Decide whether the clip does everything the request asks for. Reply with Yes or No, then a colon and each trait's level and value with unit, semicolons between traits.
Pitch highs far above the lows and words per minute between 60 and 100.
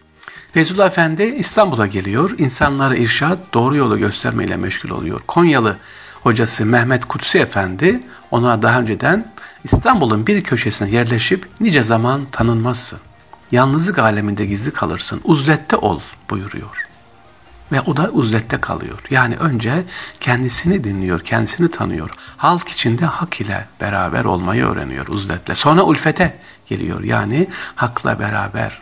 No: wide, 6.6 semitones; average, 120 wpm